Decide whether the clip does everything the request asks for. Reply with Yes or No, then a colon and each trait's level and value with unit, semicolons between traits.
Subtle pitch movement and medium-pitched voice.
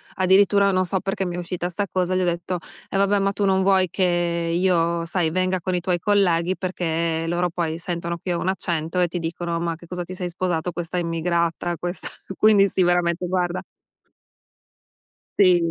Yes: narrow, 1.7 semitones; medium, 180 Hz